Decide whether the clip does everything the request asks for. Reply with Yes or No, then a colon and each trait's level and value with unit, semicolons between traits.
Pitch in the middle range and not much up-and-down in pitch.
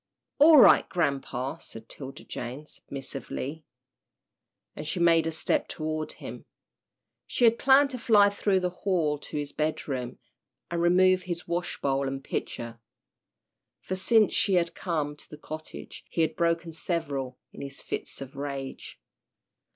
No: medium, 160 Hz; average, 4.7 semitones